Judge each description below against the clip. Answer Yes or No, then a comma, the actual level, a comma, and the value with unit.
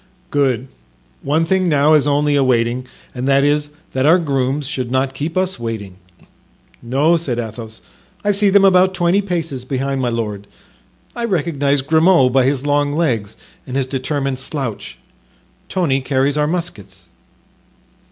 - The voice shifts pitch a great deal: No, average, 4.0 semitones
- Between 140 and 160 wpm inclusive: Yes, average, 150 wpm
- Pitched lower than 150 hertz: Yes, medium, 140 Hz